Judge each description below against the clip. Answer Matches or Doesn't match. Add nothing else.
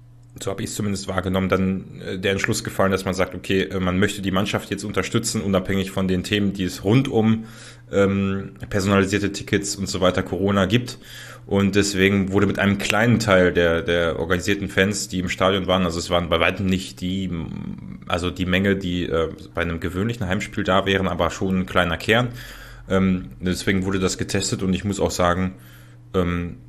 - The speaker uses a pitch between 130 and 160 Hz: Doesn't match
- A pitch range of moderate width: Doesn't match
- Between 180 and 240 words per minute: Matches